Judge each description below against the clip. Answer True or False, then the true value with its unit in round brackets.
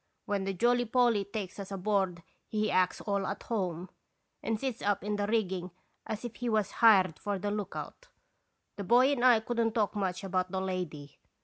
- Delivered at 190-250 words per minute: True (195 wpm)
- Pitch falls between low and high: False (205 Hz)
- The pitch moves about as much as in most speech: True (3.1 semitones)